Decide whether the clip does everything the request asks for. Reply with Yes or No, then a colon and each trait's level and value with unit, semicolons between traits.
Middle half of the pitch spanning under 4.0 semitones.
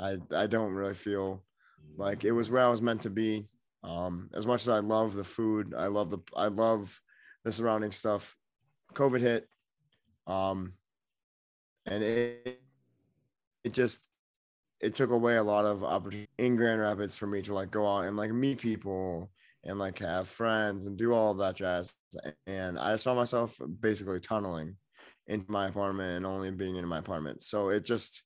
Yes: average, 3.1 semitones